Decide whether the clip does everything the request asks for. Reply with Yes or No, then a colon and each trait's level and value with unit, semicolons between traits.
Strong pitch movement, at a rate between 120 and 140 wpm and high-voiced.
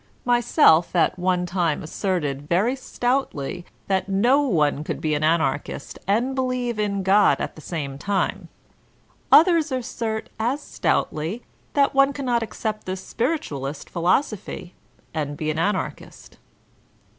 Yes: wide, 7.3 semitones; slow, 135 wpm; high, 195 Hz